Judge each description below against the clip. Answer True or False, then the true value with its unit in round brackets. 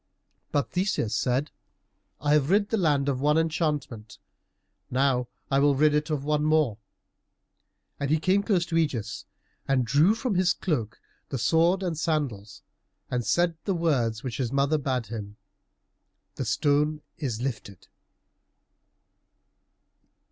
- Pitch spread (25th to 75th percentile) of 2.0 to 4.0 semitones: False (4.4 semitones)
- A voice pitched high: False (145 Hz)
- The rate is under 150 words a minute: True (140 wpm)